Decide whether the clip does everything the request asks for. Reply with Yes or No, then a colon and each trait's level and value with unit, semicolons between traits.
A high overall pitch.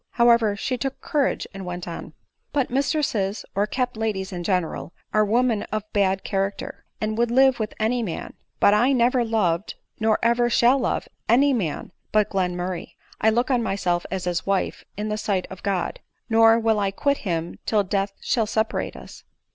Yes: high, 215 Hz